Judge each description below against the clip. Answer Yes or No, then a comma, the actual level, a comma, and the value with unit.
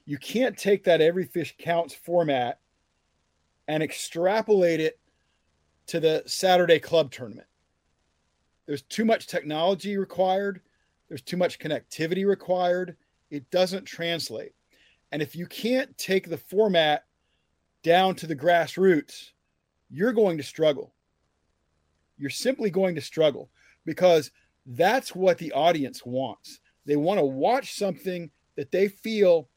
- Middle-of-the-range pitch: Yes, medium, 165 Hz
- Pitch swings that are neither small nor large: No, wide, 6.5 semitones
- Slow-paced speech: Yes, slow, 130 wpm